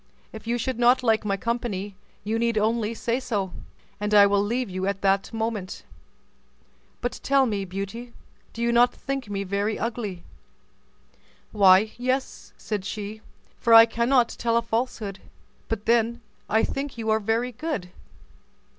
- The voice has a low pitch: No, high, 225 Hz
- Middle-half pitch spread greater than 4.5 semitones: No, average, 2.8 semitones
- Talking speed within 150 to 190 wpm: Yes, average, 155 wpm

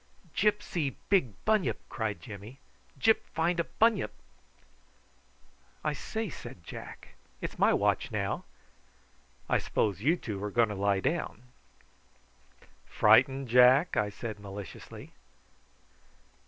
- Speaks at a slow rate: Yes, slow, 115 wpm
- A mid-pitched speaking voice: No, low, 125 Hz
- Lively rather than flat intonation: Yes, wide, 8.6 semitones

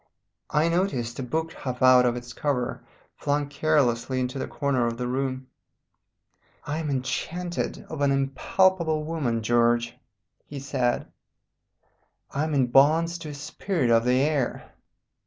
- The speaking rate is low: No, average, 145 wpm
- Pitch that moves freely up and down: No, average, 3.9 semitones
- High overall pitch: No, low, 135 Hz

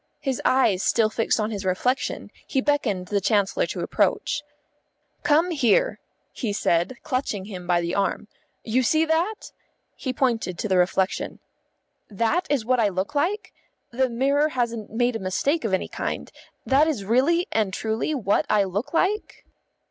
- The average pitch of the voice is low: No, high, 235 Hz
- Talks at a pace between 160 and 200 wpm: Yes, average, 165 wpm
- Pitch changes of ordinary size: No, wide, 6.2 semitones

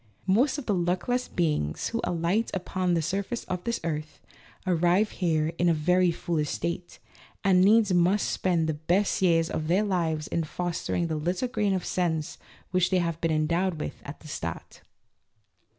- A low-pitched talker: No, medium, 175 Hz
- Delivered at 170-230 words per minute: Yes, average, 175 wpm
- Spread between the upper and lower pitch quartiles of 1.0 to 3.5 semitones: Yes, average, 2.8 semitones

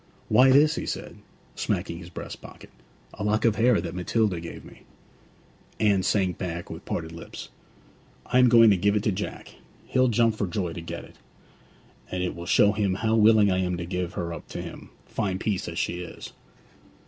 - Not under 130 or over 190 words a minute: No, average, 200 wpm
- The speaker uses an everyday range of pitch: Yes, average, 3.9 semitones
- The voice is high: No, low, 100 Hz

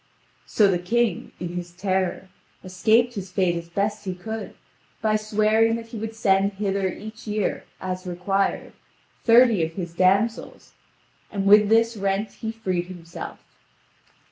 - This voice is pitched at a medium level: No, high, 200 Hz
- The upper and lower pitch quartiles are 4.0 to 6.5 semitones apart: No, average, 3.2 semitones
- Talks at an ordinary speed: Yes, average, 145 wpm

